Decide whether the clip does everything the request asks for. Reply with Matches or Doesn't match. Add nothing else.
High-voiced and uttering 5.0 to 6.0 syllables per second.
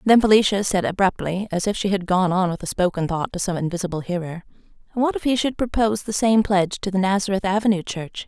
Doesn't match